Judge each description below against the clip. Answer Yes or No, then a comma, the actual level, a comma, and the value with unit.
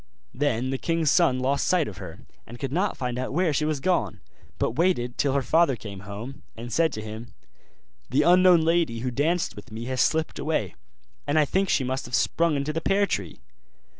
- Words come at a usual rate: No, fast, 210 wpm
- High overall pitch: No, low, 135 Hz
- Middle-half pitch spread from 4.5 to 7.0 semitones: Yes, wide, 5.4 semitones